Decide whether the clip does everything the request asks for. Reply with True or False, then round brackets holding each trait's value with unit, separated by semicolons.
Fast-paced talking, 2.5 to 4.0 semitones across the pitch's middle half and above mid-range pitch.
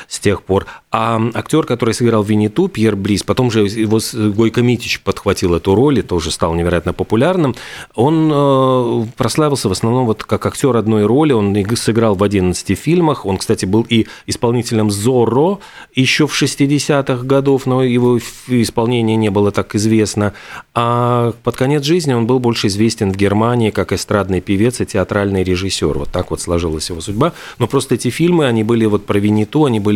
False (175 wpm; 3.6 semitones; 110 Hz)